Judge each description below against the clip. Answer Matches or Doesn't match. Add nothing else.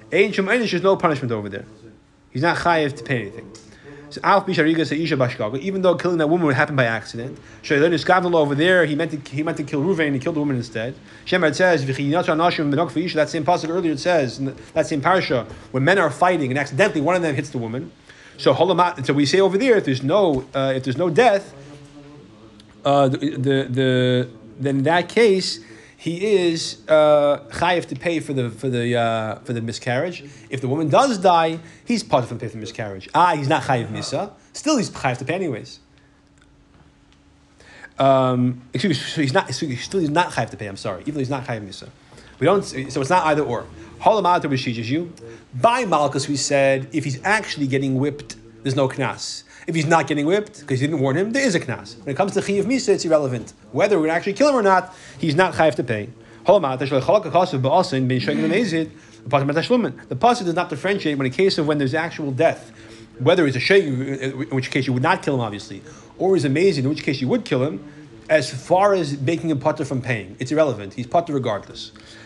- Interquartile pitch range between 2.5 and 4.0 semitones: Doesn't match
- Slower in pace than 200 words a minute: Doesn't match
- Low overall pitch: Doesn't match